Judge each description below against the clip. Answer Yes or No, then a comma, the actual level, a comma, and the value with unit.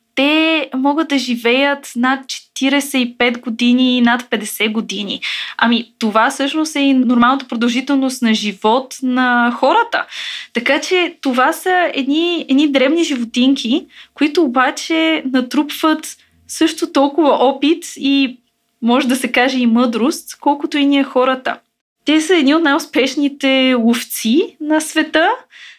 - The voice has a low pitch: No, very high, 270 Hz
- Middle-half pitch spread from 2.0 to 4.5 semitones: Yes, average, 3.7 semitones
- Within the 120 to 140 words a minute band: Yes, average, 130 wpm